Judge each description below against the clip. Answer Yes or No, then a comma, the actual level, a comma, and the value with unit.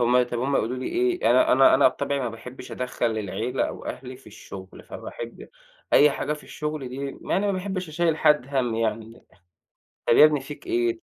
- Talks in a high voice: No, low, 135 Hz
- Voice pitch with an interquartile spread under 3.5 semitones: No, average, 4.3 semitones